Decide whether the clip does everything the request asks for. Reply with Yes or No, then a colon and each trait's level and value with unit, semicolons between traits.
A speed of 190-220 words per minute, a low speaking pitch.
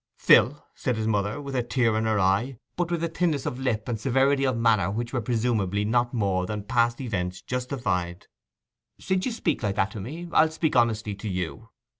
Yes: fast, 205 wpm; low, 115 Hz